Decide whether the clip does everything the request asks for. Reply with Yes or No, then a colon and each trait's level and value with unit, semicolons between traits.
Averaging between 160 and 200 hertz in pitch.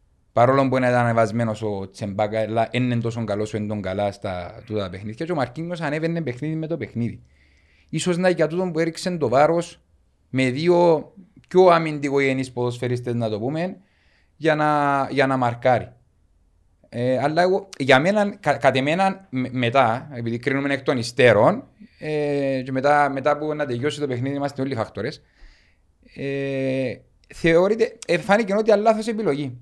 No: low, 135 Hz